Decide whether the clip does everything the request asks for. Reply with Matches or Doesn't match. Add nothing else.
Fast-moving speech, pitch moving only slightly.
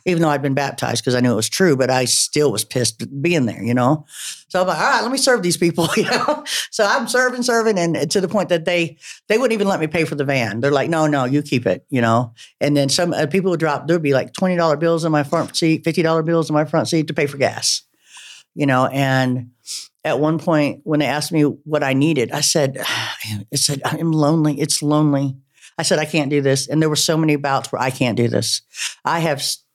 Doesn't match